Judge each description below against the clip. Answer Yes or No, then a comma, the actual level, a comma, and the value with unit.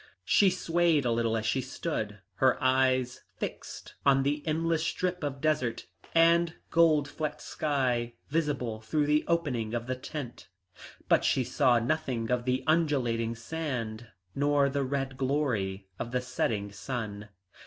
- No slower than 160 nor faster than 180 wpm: No, average, 145 wpm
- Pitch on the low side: Yes, low, 130 Hz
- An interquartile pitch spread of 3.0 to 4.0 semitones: No, average, 4.5 semitones